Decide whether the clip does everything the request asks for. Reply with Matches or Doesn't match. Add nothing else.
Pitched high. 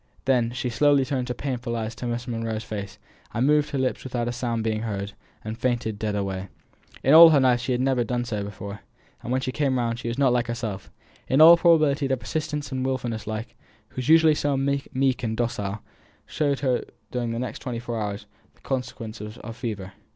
Doesn't match